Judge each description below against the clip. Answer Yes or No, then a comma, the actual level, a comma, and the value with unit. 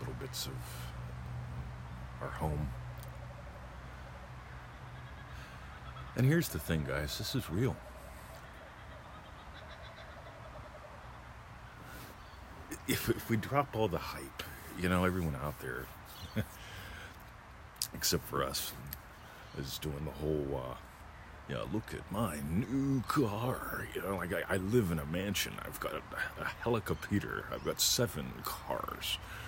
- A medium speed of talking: No, slow, 120 wpm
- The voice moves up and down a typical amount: No, wide, 7.9 semitones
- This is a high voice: No, very low, 75 Hz